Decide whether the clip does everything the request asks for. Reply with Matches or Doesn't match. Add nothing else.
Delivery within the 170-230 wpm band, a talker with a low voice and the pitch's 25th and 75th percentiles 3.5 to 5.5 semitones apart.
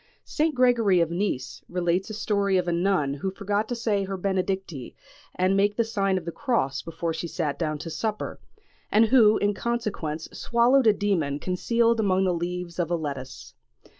Doesn't match